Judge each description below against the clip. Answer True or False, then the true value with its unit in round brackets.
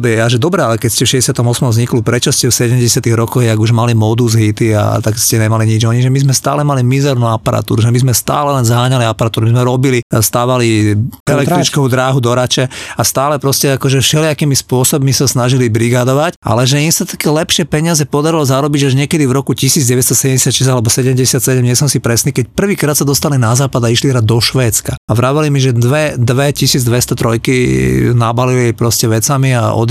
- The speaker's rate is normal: False (200 wpm)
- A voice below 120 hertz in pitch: False (130 Hz)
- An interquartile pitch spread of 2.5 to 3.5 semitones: True (2.9 semitones)